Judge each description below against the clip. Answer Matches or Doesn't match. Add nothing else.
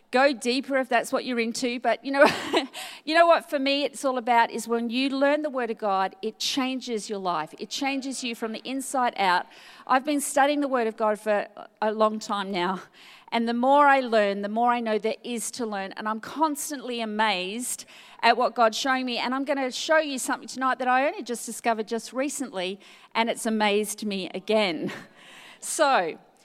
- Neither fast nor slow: Doesn't match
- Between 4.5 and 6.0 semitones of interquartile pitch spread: Doesn't match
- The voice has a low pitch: Doesn't match